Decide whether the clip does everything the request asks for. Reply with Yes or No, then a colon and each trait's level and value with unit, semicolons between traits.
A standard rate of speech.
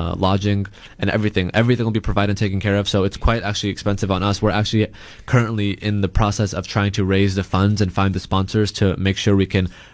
No: fast, 240 wpm